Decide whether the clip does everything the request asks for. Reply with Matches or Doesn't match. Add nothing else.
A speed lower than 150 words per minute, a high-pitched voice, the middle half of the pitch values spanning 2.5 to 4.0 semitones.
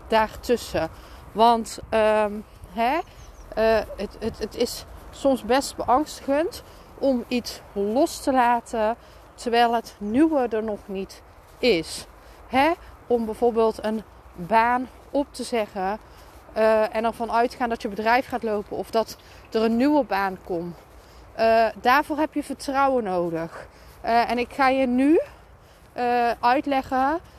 Matches